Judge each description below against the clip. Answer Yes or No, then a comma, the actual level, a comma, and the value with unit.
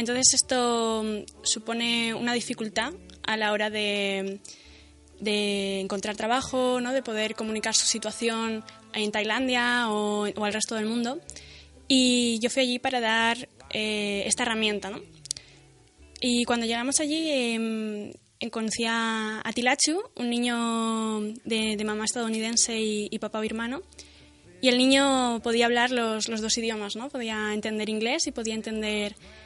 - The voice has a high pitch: Yes, high, 225 Hz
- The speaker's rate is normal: Yes, average, 145 wpm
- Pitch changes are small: Yes, narrow, 2.2 semitones